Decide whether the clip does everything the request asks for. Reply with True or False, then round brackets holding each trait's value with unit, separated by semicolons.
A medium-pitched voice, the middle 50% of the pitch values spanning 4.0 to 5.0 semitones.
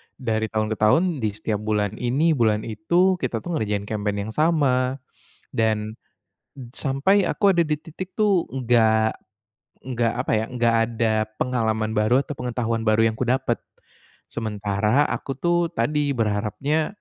False (115 Hz; 4.7 semitones)